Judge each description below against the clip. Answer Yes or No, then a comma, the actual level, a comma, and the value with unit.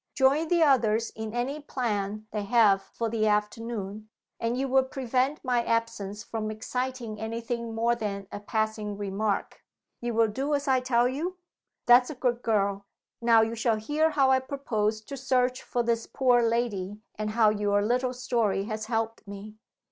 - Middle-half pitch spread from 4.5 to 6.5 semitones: No, average, 2.9 semitones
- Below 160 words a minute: No, average, 175 wpm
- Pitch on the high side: Yes, high, 230 Hz